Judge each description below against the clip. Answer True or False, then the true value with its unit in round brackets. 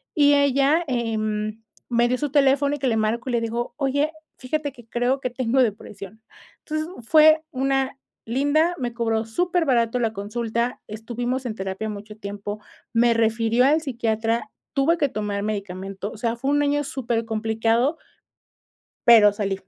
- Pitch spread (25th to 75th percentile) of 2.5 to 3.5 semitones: False (3.9 semitones)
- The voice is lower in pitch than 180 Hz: False (235 Hz)